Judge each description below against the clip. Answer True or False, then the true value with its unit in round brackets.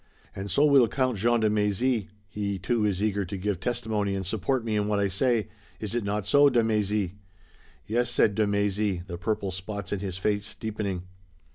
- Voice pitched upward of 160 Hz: False (105 Hz)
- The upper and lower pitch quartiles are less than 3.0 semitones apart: True (2.4 semitones)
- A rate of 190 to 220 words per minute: True (200 wpm)